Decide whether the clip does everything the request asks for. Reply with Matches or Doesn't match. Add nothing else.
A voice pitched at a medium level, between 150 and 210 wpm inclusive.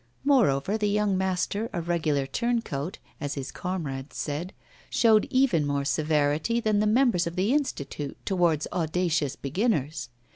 Doesn't match